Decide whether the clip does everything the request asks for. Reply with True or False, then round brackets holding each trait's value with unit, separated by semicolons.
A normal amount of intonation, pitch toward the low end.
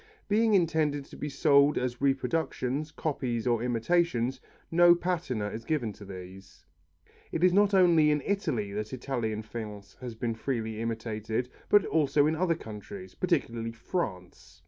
False (6.6 semitones; 130 Hz)